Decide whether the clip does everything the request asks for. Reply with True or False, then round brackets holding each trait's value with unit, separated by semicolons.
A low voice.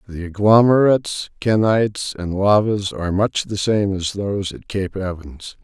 True (100 Hz)